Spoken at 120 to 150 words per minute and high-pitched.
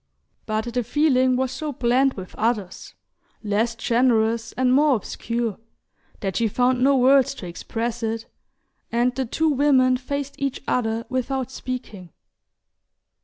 Yes: slow, 135 wpm; high, 245 Hz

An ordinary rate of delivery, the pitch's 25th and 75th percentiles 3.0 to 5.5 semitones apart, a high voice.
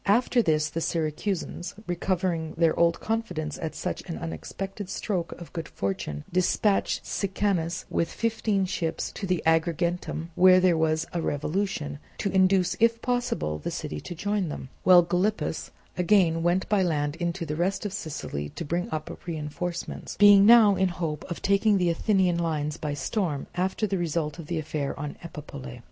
No: average, 165 wpm; average, 3.6 semitones; medium, 175 Hz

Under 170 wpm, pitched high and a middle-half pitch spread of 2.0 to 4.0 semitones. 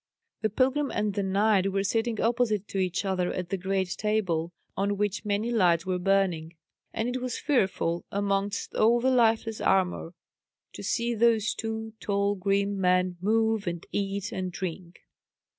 Yes: average, 160 wpm; high, 200 Hz; average, 3.0 semitones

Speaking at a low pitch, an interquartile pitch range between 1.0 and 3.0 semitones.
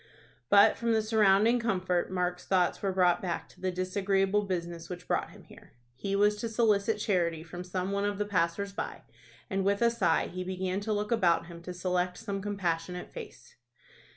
No: high, 190 Hz; narrow, 2.5 semitones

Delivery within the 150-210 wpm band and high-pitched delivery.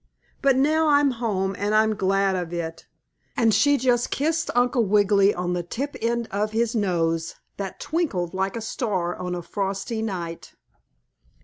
Yes: average, 165 wpm; high, 205 Hz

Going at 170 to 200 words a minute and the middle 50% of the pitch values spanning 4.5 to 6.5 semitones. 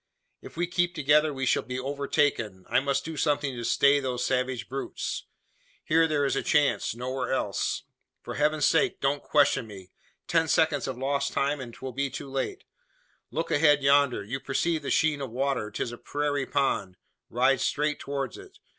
No: average, 180 wpm; narrow, 2.4 semitones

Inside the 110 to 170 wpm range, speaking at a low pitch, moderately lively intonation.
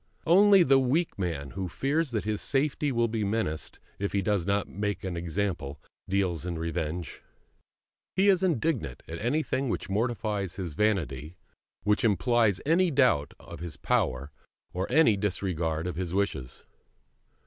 No: average, 150 wpm; low, 100 Hz; wide, 6.8 semitones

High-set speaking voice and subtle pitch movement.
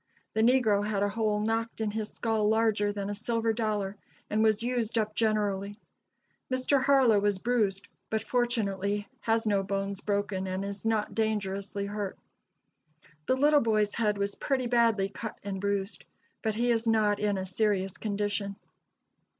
Yes: high, 210 Hz; narrow, 2.0 semitones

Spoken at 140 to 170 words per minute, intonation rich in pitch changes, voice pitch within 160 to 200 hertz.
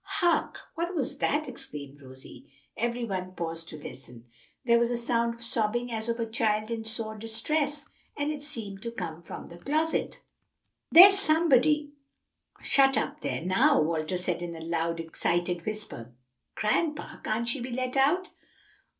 No: average, 160 wpm; wide, 8.2 semitones; high, 230 Hz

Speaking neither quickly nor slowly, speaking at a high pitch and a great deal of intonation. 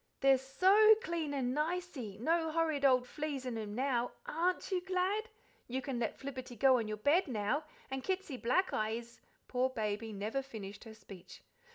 Yes: average, 180 wpm; very high, 265 Hz; wide, 6.2 semitones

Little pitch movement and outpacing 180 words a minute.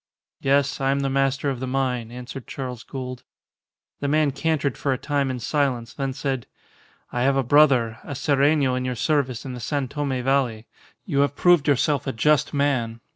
Yes: narrow, 2.1 semitones; average, 190 wpm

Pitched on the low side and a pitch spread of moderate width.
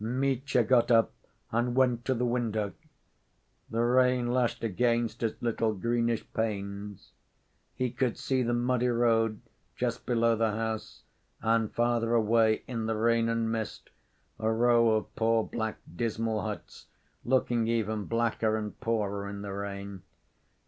No: low, 115 Hz; narrow, 1.6 semitones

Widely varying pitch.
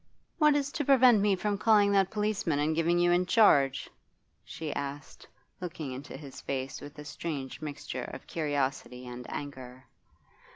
Yes: wide, 6.6 semitones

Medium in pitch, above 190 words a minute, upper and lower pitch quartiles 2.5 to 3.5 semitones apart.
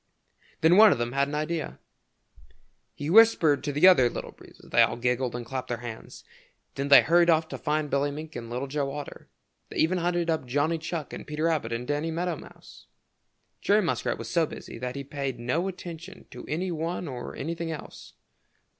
No: medium, 150 Hz; average, 200 wpm; average, 4.0 semitones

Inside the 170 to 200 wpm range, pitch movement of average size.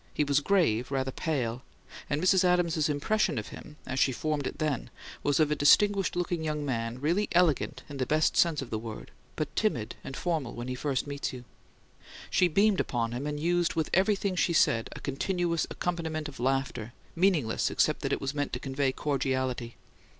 Yes: average, 195 wpm; average, 4.6 semitones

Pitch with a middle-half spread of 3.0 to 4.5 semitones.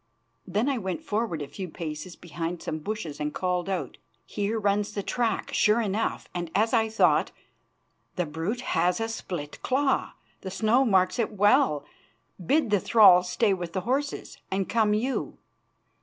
Yes: average, 4.1 semitones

